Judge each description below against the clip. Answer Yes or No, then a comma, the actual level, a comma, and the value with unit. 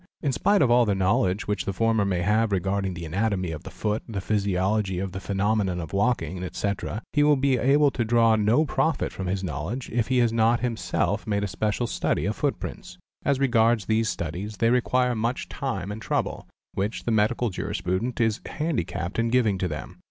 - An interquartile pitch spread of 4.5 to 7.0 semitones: No, average, 3.8 semitones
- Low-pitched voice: Yes, low, 110 Hz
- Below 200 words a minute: No, fast, 205 wpm